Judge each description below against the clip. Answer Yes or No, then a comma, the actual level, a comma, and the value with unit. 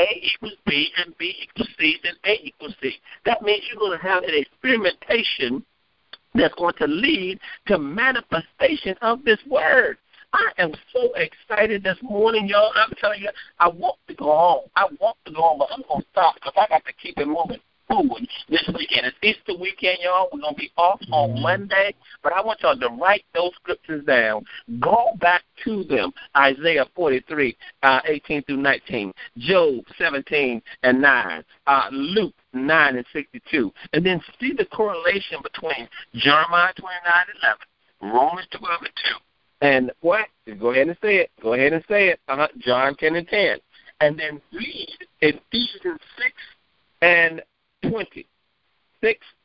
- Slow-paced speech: No, average, 165 wpm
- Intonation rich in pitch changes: Yes, wide, 6.7 semitones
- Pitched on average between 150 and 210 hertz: Yes, medium, 185 Hz